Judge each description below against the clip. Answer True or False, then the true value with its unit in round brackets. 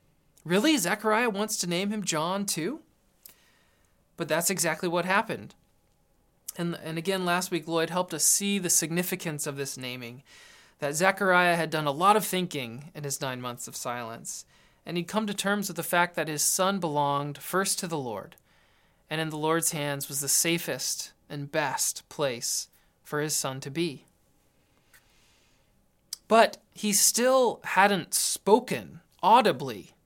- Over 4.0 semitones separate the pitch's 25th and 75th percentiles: True (4.6 semitones)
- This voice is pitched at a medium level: True (165 Hz)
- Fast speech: False (160 wpm)